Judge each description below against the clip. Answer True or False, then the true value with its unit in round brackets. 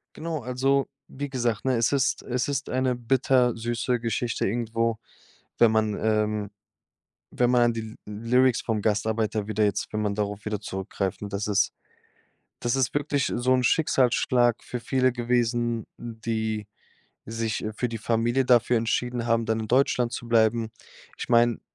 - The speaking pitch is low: True (115 Hz)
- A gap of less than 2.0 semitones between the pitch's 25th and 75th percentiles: False (2.3 semitones)